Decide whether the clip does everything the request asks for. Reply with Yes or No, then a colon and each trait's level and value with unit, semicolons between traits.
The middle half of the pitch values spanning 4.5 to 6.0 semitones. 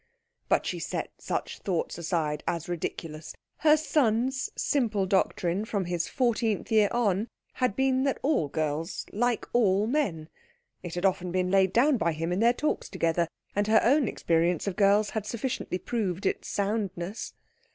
Yes: average, 5.2 semitones